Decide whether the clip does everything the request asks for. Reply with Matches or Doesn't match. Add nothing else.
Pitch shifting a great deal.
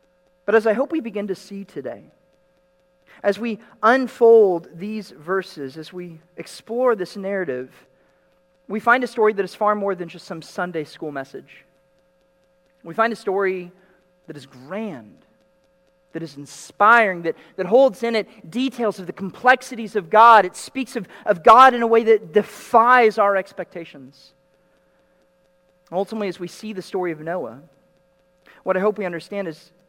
Doesn't match